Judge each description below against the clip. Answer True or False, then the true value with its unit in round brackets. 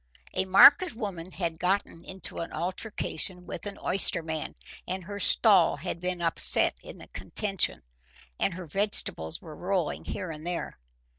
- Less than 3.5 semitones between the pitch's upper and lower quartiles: True (2.9 semitones)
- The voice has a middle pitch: True (180 Hz)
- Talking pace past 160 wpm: False (150 wpm)